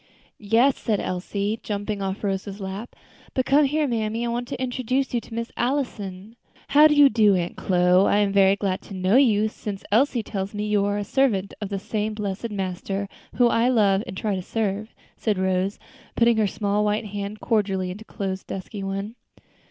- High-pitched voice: Yes, high, 210 Hz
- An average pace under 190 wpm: No, average, 195 wpm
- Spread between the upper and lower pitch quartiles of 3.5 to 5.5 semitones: No, average, 2.9 semitones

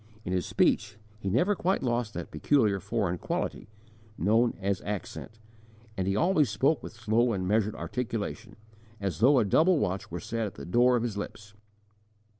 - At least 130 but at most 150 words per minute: No, average, 175 wpm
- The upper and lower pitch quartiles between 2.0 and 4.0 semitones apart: Yes, average, 3.7 semitones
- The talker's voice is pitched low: Yes, low, 110 Hz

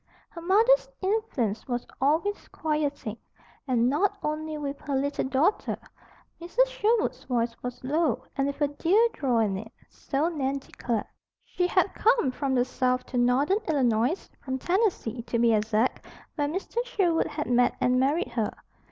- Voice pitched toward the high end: Yes, very high, 280 Hz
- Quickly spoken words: No, average, 160 wpm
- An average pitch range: No, wide, 5.8 semitones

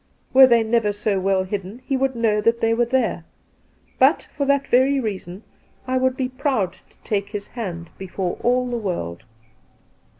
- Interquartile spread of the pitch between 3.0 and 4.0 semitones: No, average, 4.7 semitones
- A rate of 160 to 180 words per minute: Yes, average, 175 wpm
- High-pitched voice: Yes, high, 230 Hz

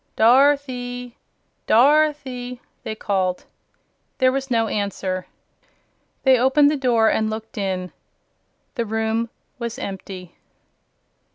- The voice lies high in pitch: Yes, high, 235 Hz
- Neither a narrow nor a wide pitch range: Yes, average, 3.6 semitones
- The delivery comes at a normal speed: No, slow, 100 wpm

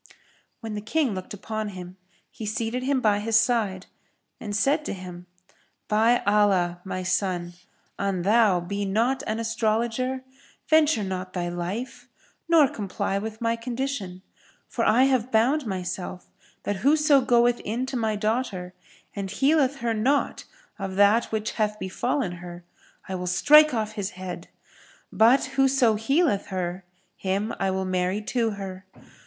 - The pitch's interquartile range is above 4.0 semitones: Yes, average, 4.5 semitones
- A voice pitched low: No, high, 215 Hz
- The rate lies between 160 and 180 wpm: No, average, 150 wpm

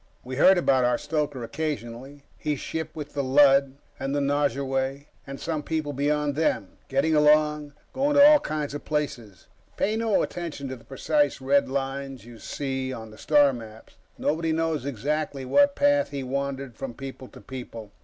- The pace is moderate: Yes, average, 175 wpm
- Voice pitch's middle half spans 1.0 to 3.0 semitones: Yes, narrow, 2.4 semitones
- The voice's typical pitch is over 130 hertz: Yes, medium, 140 Hz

